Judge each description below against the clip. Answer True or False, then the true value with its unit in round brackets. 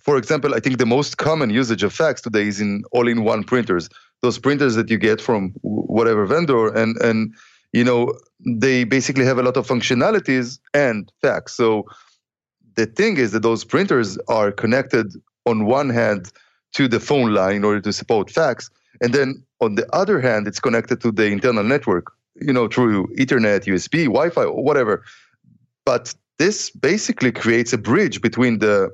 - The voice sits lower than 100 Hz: False (115 Hz)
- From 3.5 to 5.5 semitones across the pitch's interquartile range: False (2.8 semitones)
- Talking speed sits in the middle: True (175 wpm)